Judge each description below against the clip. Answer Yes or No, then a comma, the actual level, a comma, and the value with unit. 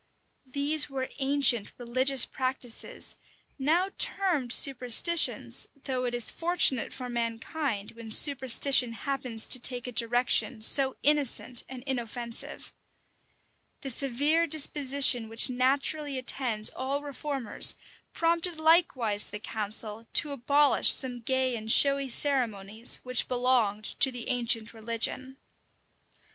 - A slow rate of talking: Yes, slow, 115 wpm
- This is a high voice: Yes, very high, 255 Hz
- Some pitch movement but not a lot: Yes, average, 3.2 semitones